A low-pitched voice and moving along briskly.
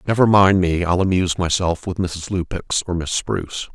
No: very low, 90 Hz; average, 190 wpm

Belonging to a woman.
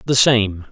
No: male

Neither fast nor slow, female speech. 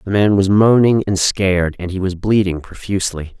No: average, 195 wpm; male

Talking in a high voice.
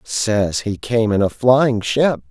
No: low, 110 Hz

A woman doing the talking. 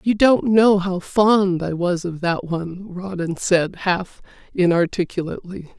Yes: female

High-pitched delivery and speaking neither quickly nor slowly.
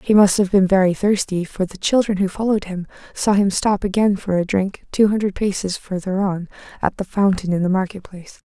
No: high, 195 Hz; fast, 220 wpm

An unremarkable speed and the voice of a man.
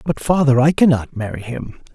Yes: average, 185 wpm; male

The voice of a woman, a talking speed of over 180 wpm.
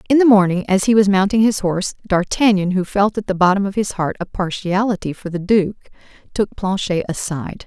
Yes: female; fast, 205 wpm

